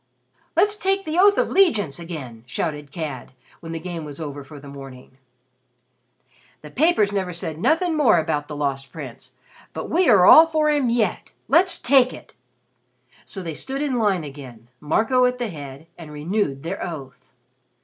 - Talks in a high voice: No, medium, 170 Hz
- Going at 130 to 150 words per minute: No, average, 170 wpm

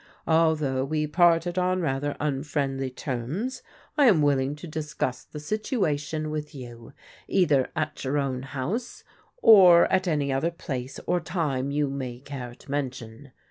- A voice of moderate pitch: Yes, medium, 145 Hz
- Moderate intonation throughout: Yes, average, 3.7 semitones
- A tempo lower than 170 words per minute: Yes, average, 145 wpm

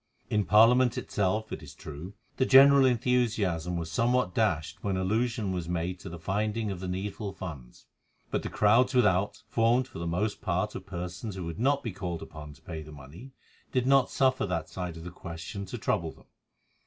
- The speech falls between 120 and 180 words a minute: No, average, 195 wpm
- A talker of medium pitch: No, very low, 95 Hz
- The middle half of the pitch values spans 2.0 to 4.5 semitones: No, average, 5.0 semitones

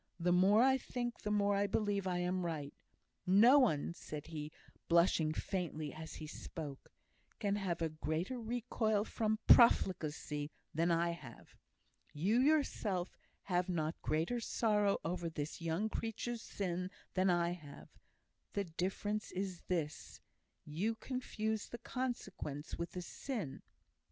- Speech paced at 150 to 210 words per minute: No, slow, 135 wpm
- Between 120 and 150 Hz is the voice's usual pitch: No, medium, 180 Hz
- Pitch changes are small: No, average, 4.9 semitones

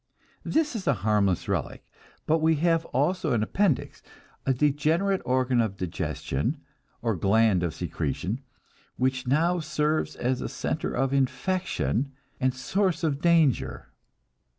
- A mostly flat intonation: No, wide, 5.5 semitones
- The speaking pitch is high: No, medium, 140 Hz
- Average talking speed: No, slow, 130 wpm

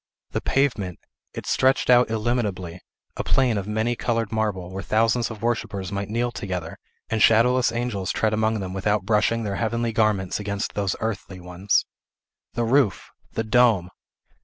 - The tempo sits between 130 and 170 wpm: Yes, average, 160 wpm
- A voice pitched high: No, low, 110 Hz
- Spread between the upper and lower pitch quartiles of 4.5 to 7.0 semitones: No, average, 3.1 semitones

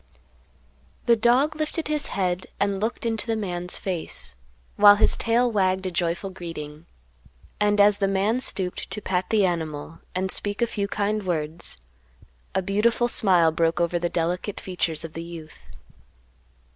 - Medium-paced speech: Yes, average, 160 wpm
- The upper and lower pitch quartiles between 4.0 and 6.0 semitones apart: No, average, 3.6 semitones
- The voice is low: No, high, 190 Hz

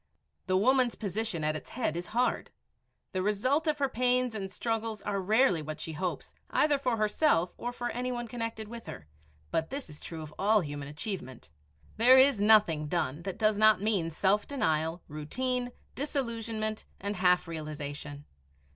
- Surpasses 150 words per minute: Yes, average, 170 wpm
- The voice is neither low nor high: No, high, 210 Hz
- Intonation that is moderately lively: No, wide, 6.6 semitones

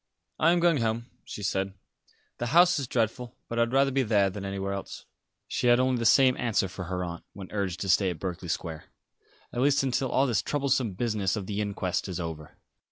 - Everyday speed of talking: No, fast, 220 wpm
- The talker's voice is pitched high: No, low, 105 Hz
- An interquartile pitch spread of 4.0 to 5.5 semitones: Yes, average, 4.9 semitones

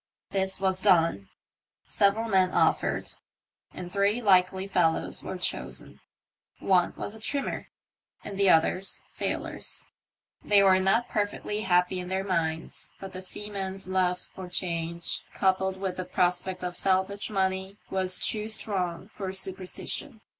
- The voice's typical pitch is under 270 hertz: Yes, high, 190 Hz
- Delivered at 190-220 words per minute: No, slow, 135 wpm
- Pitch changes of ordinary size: No, narrow, 1.6 semitones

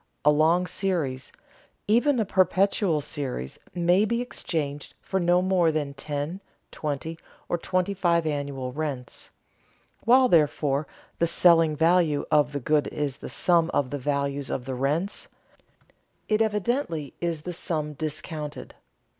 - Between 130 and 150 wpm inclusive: Yes, average, 140 wpm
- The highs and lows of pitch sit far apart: No, average, 3.9 semitones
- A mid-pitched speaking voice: Yes, medium, 160 Hz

